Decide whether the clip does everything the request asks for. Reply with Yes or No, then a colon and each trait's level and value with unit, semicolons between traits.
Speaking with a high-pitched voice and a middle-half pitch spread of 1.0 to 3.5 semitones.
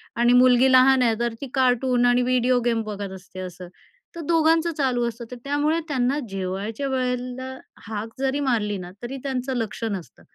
Yes: high, 245 Hz; average, 2.9 semitones